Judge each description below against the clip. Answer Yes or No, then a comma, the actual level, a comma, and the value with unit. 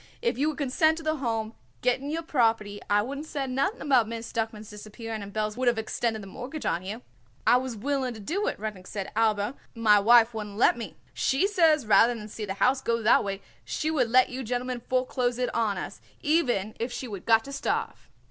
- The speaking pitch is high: Yes, high, 235 Hz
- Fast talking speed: Yes, fast, 220 wpm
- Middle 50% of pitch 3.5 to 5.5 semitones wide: Yes, average, 3.8 semitones